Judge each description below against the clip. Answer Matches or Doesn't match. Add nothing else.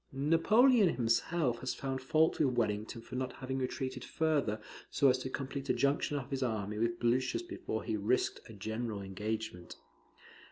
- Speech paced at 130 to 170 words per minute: Matches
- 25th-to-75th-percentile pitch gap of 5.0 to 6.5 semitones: Doesn't match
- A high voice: Doesn't match